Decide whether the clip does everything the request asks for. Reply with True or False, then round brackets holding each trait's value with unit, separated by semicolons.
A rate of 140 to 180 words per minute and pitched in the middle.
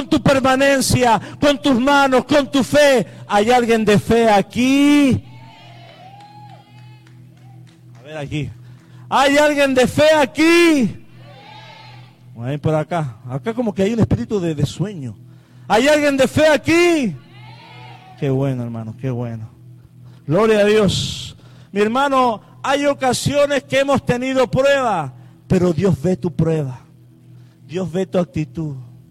False (130 wpm; 165 Hz)